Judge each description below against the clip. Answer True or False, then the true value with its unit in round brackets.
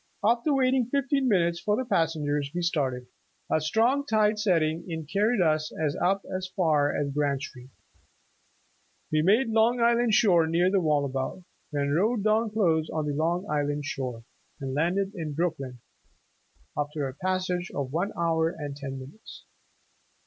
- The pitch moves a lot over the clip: True (6.2 semitones)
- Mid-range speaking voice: True (170 Hz)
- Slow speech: False (155 wpm)